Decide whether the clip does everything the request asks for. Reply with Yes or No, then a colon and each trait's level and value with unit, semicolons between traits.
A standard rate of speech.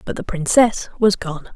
Yes: average, 195 wpm